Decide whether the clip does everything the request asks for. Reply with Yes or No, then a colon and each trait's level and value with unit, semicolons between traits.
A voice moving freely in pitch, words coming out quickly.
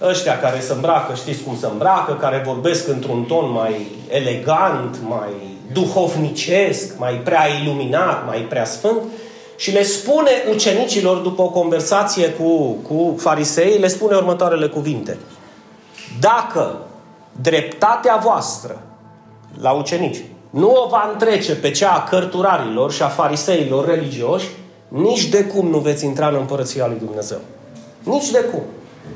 No: wide, 5.8 semitones; average, 135 wpm